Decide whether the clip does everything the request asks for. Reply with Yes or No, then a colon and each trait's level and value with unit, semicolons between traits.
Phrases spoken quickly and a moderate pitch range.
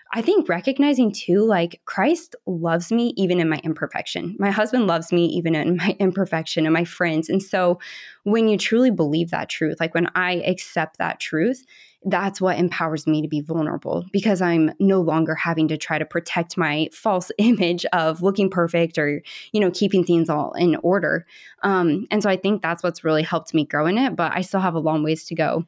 Yes: fast, 210 wpm; average, 3.5 semitones